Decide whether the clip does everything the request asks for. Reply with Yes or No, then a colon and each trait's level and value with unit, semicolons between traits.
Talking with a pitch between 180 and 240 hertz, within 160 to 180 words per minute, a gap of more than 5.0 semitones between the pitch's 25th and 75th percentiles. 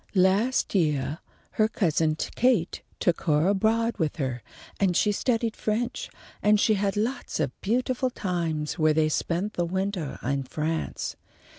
No: high, 190 Hz; average, 145 wpm; wide, 5.6 semitones